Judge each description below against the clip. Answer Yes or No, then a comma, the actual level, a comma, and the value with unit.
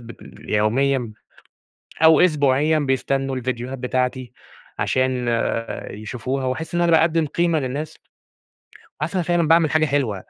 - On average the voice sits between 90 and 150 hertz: Yes, low, 135 Hz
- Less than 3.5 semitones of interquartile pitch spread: No, average, 3.8 semitones